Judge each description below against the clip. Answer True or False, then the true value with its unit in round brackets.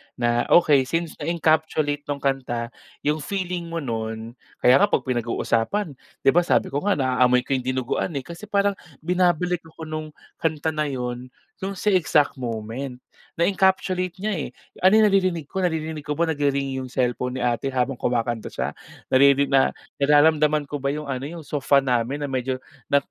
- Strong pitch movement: False (4.7 semitones)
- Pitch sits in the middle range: True (145 Hz)